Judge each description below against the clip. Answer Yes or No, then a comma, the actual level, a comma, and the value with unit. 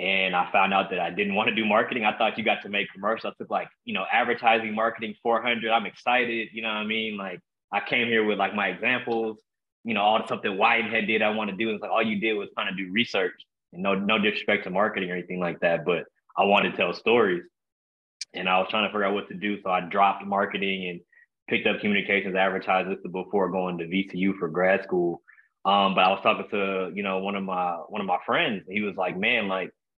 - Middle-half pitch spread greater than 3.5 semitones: No, average, 2.8 semitones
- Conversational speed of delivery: No, fast, 250 wpm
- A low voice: Yes, low, 100 Hz